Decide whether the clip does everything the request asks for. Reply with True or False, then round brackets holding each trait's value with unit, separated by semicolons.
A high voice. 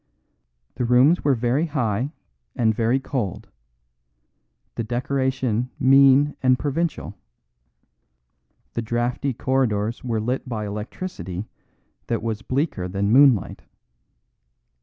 False (125 Hz)